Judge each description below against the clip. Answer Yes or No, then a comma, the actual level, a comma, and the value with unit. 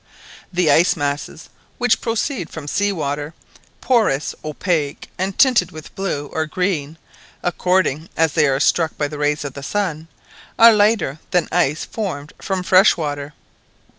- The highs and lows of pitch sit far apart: No, average, 4.6 semitones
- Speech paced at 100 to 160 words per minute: Yes, average, 150 wpm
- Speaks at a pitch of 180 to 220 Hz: No, medium, 165 Hz